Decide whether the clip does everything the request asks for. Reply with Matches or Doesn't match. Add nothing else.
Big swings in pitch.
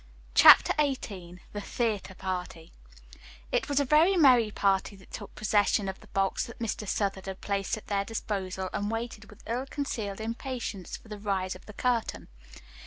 Doesn't match